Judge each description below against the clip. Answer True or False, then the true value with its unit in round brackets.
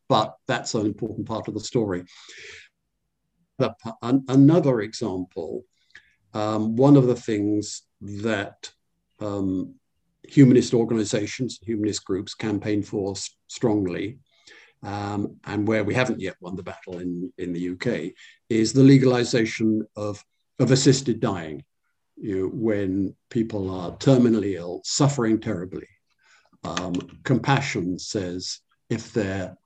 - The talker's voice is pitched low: True (110 Hz)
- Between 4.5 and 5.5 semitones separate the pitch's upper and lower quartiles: False (3.7 semitones)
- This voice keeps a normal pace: False (120 wpm)